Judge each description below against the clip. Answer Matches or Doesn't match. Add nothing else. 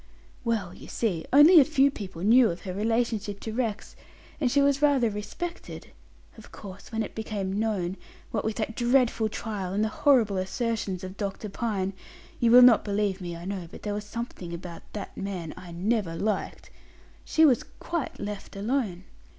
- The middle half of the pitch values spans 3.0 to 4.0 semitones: Matches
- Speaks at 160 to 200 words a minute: Matches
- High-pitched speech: Matches